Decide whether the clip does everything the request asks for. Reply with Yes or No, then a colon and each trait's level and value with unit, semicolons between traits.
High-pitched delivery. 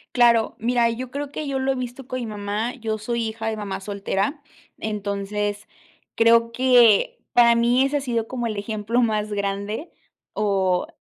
Yes: high, 230 Hz